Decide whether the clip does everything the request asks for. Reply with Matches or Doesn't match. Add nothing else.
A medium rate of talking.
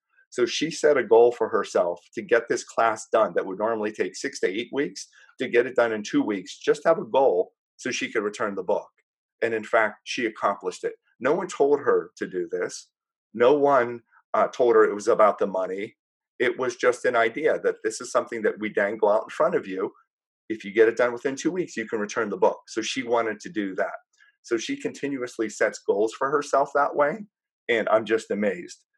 Doesn't match